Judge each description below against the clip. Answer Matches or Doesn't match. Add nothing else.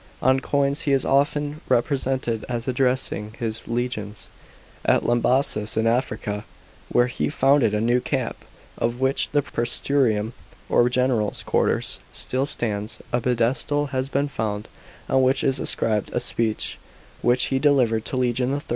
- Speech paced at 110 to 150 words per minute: Matches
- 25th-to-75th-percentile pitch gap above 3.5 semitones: Doesn't match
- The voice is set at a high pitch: Doesn't match